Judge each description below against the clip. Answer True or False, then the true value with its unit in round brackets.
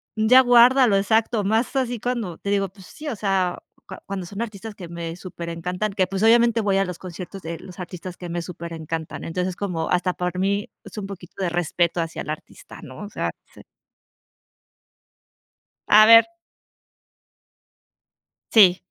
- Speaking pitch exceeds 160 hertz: True (190 Hz)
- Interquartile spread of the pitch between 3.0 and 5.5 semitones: True (3.7 semitones)